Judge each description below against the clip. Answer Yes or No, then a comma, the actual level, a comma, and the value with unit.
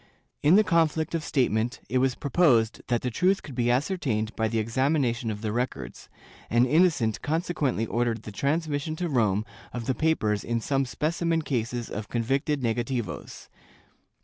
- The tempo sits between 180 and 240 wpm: No, average, 160 wpm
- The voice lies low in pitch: Yes, low, 125 Hz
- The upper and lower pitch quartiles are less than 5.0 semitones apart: No, average, 5.3 semitones